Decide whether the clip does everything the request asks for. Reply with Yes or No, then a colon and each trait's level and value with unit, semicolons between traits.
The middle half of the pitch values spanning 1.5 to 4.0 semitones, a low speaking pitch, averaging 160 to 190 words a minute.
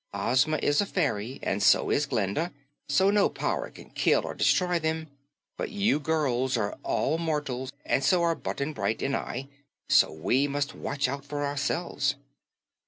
No: average, 3.5 semitones; medium, 145 Hz; average, 170 wpm